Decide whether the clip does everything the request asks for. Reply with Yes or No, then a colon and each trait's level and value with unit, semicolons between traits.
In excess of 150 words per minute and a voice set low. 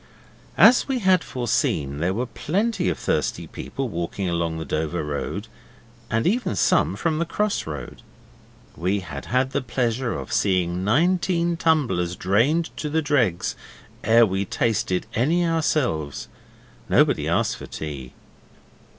No: average, 140 wpm; low, 115 Hz